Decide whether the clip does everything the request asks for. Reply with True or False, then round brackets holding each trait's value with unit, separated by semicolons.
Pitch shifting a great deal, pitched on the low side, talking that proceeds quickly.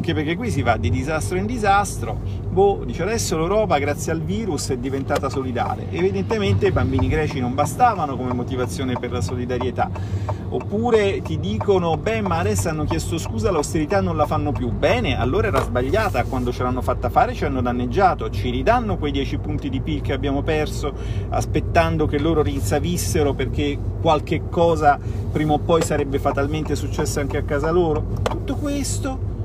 True (6.8 semitones; 125 Hz; 175 wpm)